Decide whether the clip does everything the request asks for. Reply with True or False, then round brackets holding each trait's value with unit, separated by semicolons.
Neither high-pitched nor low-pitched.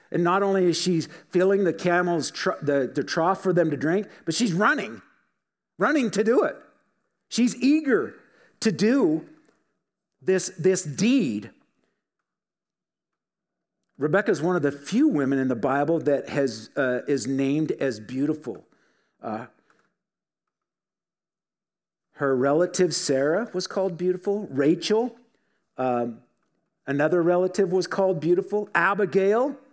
True (180 Hz)